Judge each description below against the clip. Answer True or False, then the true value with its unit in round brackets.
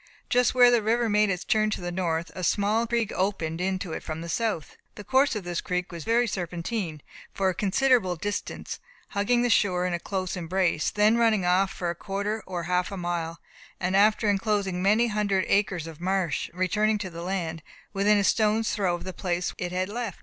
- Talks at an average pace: False (210 wpm)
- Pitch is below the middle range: False (195 Hz)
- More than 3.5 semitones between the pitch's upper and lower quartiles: False (3.2 semitones)